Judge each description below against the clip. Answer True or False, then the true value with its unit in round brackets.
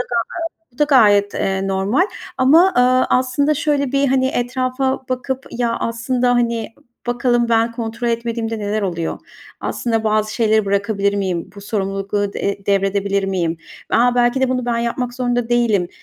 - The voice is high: True (230 Hz)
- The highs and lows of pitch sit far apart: False (3.8 semitones)